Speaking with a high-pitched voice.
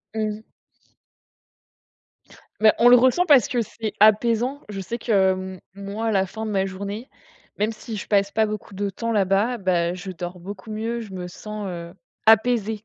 Yes: high, 210 Hz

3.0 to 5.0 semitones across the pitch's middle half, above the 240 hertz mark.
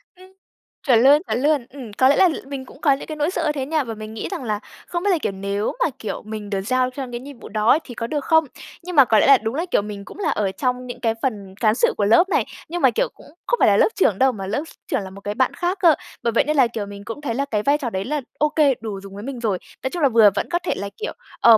No: wide, 5.5 semitones; very high, 250 Hz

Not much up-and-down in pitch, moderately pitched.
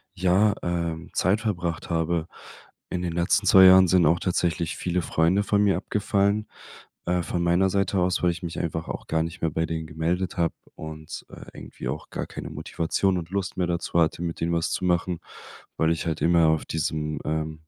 No: narrow, 2.2 semitones; very low, 85 Hz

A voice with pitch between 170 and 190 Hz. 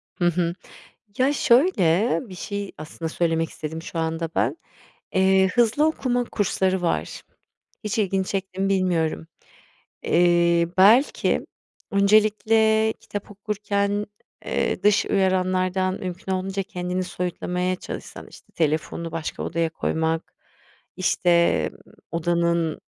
Yes: medium, 185 Hz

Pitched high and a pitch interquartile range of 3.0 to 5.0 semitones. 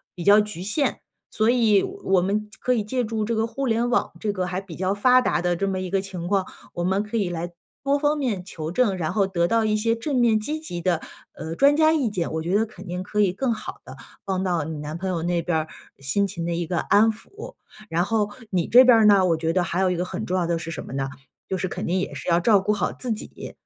Yes: high, 195 Hz; average, 4.3 semitones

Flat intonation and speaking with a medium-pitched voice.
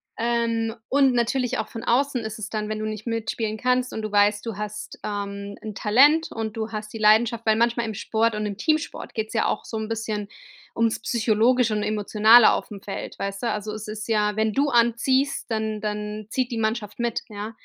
No: narrow, 1.8 semitones; high, 220 Hz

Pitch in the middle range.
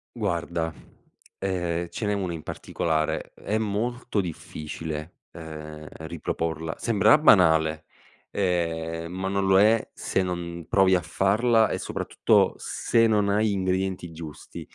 No: very low, 90 Hz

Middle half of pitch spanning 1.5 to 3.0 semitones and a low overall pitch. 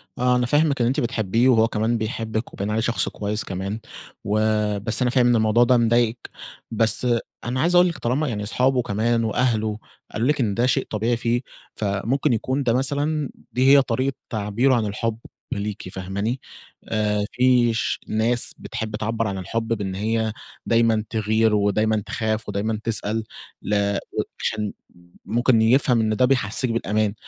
Yes: narrow, 2.5 semitones; low, 115 Hz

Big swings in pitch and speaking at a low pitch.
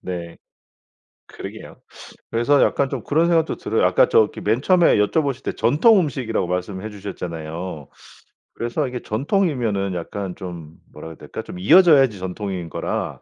Yes: wide, 7.5 semitones; low, 105 Hz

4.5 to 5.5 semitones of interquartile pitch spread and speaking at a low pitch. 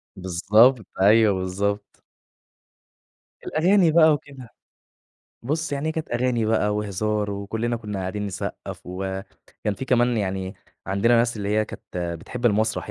No: average, 3.6 semitones; low, 110 Hz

